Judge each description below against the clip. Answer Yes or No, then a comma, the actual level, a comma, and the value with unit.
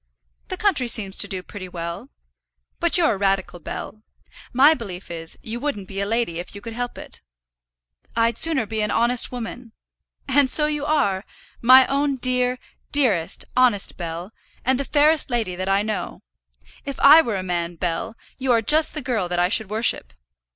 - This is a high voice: Yes, high, 230 Hz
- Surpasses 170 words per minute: Yes, average, 185 wpm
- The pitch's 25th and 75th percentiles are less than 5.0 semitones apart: No, wide, 5.6 semitones